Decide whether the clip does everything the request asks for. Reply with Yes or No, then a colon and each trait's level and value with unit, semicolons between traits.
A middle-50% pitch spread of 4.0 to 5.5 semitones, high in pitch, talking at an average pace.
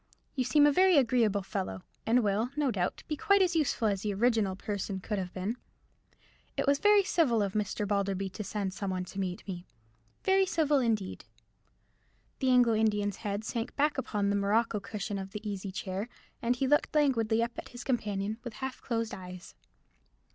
Yes: average, 4.3 semitones; high, 215 Hz; average, 185 wpm